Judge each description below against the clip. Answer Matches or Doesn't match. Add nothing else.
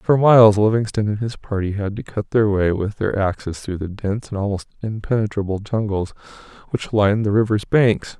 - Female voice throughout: Doesn't match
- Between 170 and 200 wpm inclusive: Matches